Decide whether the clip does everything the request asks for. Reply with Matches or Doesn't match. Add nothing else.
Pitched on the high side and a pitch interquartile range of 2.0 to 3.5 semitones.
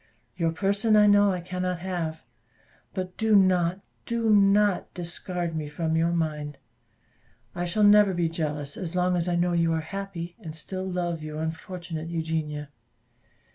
Doesn't match